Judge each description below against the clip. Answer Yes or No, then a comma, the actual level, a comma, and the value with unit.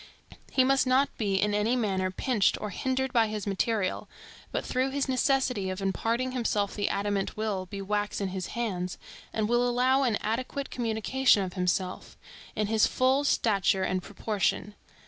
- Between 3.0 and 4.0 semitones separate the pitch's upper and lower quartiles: No, average, 4.5 semitones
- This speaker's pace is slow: No, average, 165 wpm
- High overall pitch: Yes, high, 215 Hz